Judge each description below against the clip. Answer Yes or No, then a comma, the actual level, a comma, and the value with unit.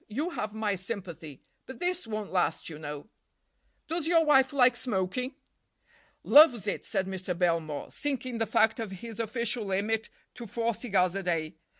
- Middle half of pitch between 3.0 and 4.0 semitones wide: No, average, 5.2 semitones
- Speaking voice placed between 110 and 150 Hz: No, high, 220 Hz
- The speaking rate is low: No, average, 165 wpm